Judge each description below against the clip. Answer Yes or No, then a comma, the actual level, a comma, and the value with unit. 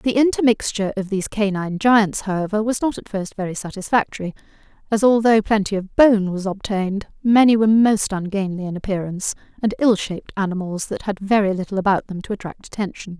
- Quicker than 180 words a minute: No, average, 175 wpm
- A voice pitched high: Yes, high, 205 Hz